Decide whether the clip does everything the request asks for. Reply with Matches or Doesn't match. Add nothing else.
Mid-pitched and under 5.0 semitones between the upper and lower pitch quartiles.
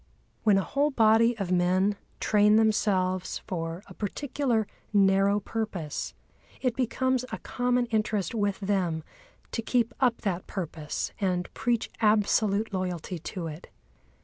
Doesn't match